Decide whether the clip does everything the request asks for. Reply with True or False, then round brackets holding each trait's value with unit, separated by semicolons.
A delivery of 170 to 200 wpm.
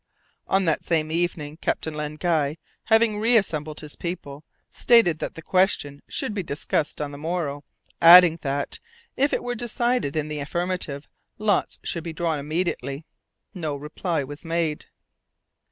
False (150 wpm)